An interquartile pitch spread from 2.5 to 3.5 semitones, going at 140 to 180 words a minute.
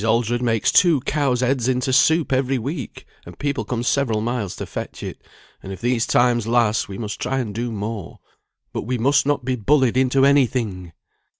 No: average, 2.9 semitones; average, 195 wpm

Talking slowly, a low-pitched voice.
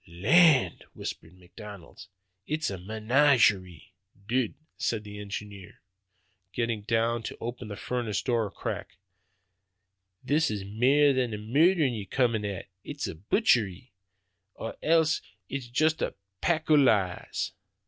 Yes: slow, 130 wpm; low, 115 Hz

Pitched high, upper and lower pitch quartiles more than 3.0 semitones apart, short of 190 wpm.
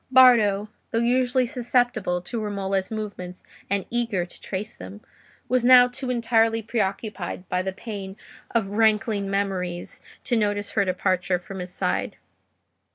Yes: high, 205 Hz; average, 3.6 semitones; average, 140 wpm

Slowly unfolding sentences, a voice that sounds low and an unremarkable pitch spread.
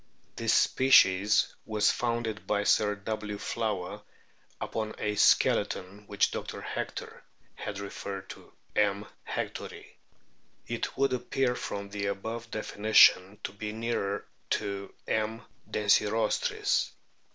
No: slow, 110 wpm; low, 105 Hz; narrow, 1.8 semitones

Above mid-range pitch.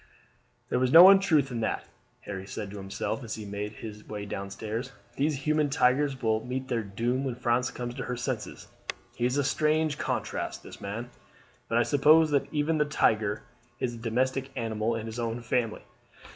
No: low, 120 Hz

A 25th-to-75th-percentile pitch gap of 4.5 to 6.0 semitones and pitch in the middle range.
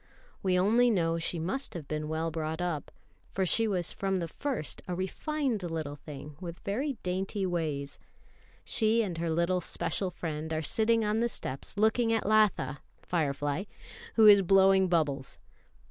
Yes: average, 4.9 semitones; medium, 180 Hz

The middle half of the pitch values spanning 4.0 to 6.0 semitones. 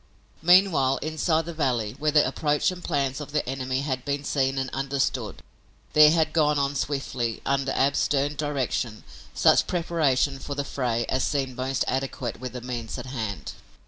No: narrow, 2.5 semitones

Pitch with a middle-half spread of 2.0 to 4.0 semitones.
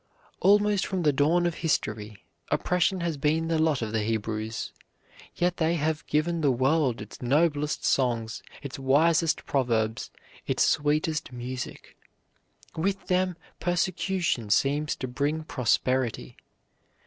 No: average, 5.1 semitones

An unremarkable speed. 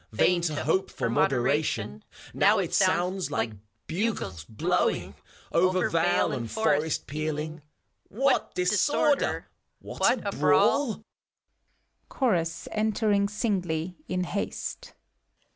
No: slow, 105 wpm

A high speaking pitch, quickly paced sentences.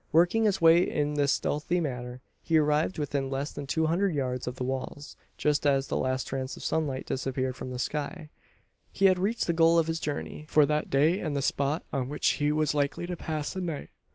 No: medium, 150 Hz; fast, 220 wpm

